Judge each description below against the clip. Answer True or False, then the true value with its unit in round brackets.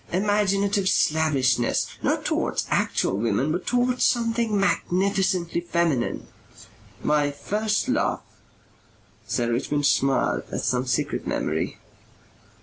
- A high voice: False (170 Hz)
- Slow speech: True (105 wpm)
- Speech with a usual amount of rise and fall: False (7.0 semitones)